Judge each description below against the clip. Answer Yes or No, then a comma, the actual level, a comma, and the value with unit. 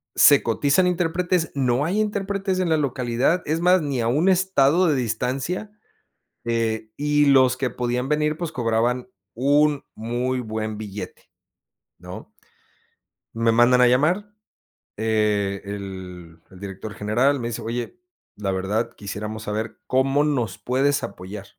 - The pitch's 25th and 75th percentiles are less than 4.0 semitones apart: No, wide, 5.4 semitones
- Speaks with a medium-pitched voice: No, low, 125 Hz